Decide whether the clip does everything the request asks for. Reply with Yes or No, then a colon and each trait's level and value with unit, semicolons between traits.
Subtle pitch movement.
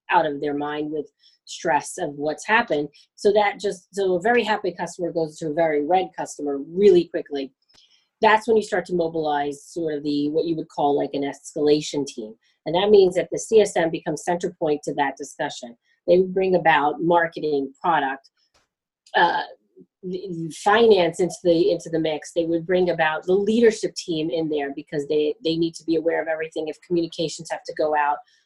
No: average, 3.4 semitones